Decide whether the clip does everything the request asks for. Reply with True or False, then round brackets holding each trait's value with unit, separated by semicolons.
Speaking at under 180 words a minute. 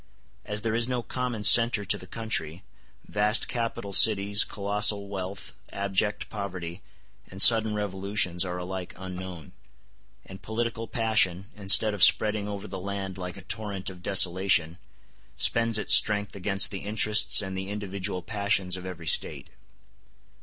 True (145 wpm)